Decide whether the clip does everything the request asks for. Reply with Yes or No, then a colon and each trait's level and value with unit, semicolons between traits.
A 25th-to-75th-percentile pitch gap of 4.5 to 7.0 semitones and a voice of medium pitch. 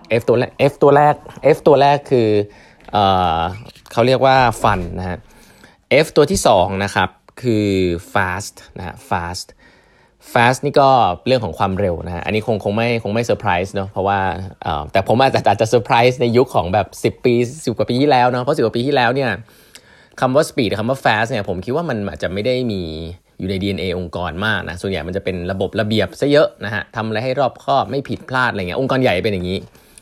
No: average, 4.8 semitones; low, 105 Hz